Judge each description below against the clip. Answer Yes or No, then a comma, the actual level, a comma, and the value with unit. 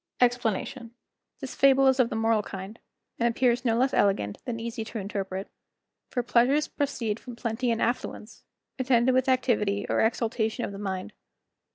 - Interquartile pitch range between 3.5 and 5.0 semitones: No, average, 2.8 semitones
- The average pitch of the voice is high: Yes, high, 235 Hz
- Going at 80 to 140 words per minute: No, average, 160 wpm